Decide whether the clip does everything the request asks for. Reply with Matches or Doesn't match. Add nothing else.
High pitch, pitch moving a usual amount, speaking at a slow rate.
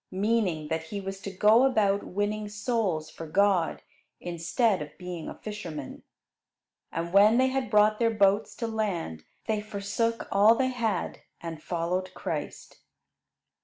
Doesn't match